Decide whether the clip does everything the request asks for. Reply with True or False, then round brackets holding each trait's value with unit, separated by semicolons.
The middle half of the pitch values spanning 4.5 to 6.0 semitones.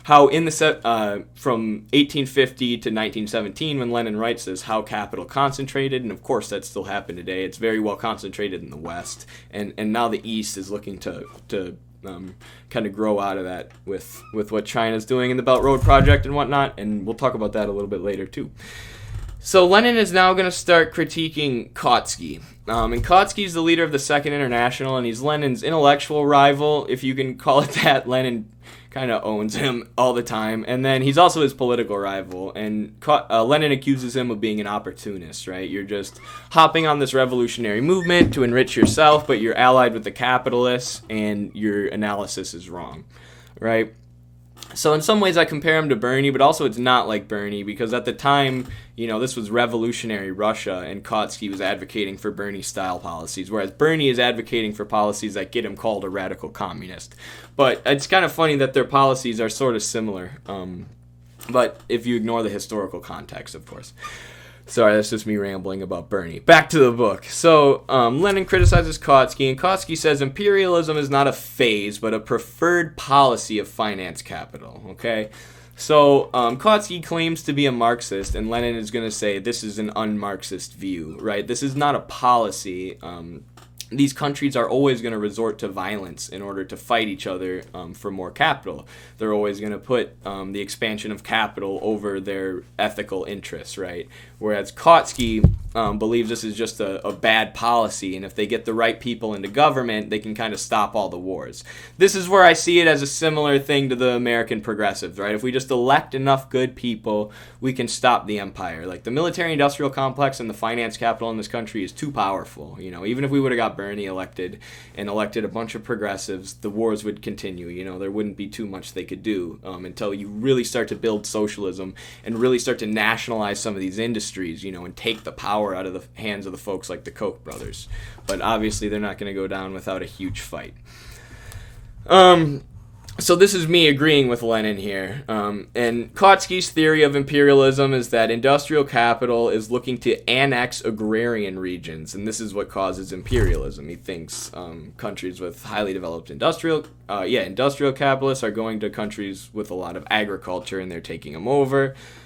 True (4.9 semitones)